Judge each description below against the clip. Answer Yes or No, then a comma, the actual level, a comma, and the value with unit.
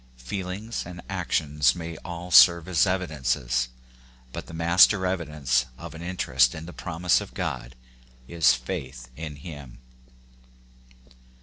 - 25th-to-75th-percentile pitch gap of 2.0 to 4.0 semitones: No, average, 5.3 semitones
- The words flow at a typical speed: No, slow, 130 wpm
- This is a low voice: Yes, very low, 80 Hz